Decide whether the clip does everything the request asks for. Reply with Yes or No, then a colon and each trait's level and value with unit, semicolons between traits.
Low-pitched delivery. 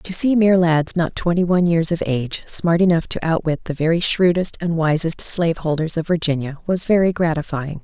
No: medium, 165 Hz